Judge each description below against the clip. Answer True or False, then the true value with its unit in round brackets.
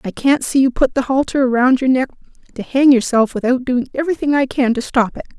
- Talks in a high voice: True (260 Hz)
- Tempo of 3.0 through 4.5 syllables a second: False (6.0 syllables/s)